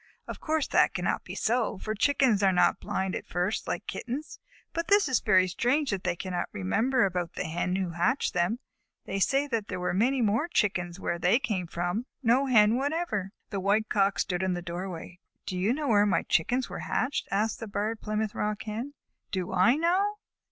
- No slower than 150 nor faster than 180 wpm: No, fast, 205 wpm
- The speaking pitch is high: Yes, high, 210 Hz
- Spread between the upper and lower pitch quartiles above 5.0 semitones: Yes, wide, 5.4 semitones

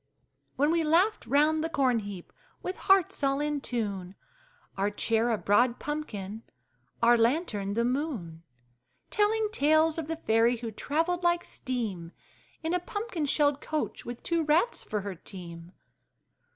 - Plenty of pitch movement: Yes, wide, 7.0 semitones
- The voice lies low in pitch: No, very high, 275 Hz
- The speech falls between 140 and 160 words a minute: Yes, average, 150 wpm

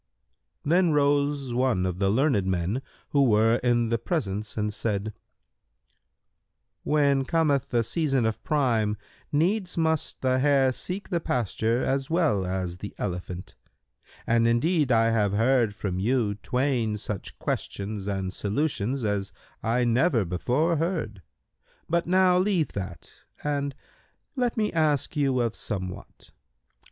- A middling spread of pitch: No, wide, 5.9 semitones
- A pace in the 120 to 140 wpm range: Yes, slow, 135 wpm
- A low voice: Yes, low, 120 Hz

